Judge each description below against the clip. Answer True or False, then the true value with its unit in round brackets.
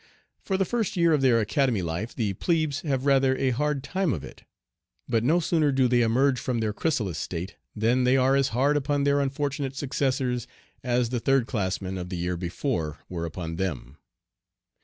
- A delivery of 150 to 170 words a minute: False (195 wpm)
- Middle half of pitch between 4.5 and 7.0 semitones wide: True (5.4 semitones)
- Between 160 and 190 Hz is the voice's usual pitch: False (130 Hz)